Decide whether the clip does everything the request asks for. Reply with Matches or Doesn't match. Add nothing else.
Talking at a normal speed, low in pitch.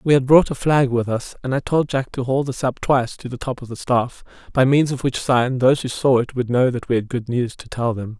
Doesn't match